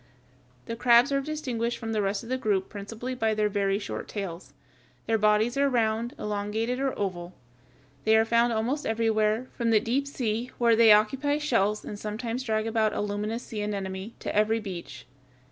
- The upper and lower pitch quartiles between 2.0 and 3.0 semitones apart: Yes, narrow, 2.4 semitones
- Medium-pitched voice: No, high, 220 Hz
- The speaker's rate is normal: Yes, average, 180 wpm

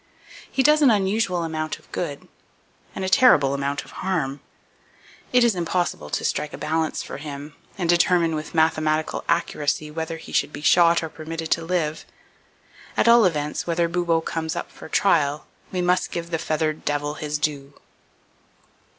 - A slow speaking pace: No, average, 170 wpm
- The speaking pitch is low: No, medium, 160 Hz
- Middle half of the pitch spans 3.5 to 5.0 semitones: No, average, 2.7 semitones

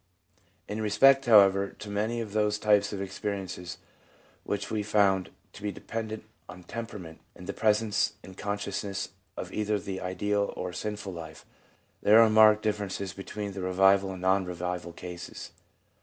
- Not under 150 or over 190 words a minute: Yes, average, 155 wpm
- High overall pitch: No, low, 100 Hz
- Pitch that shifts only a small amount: Yes, narrow, 2.1 semitones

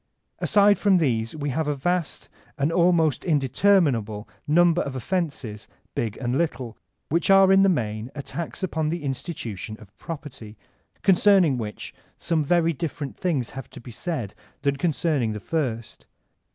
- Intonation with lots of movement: Yes, wide, 6.2 semitones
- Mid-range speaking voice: Yes, medium, 150 Hz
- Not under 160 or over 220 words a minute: No, average, 150 wpm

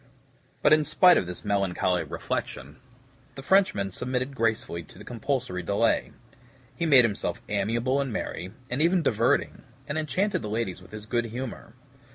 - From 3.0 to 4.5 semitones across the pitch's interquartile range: No, wide, 5.5 semitones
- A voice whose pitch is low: Yes, low, 115 Hz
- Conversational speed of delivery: Yes, average, 160 wpm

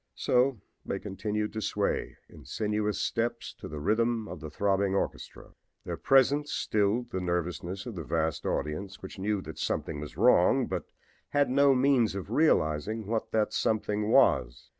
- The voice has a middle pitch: No, low, 105 Hz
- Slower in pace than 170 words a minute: Yes, average, 160 wpm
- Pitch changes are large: No, average, 3.9 semitones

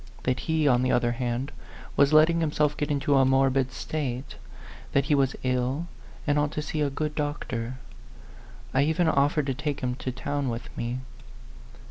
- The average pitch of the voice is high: No, medium, 140 Hz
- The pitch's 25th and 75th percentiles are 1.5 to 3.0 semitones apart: Yes, average, 2.7 semitones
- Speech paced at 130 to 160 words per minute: No, average, 175 wpm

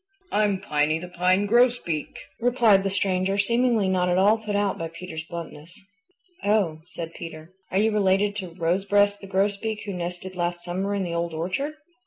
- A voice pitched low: No, high, 190 Hz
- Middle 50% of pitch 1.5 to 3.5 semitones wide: Yes, average, 2.9 semitones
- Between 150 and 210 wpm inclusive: Yes, average, 175 wpm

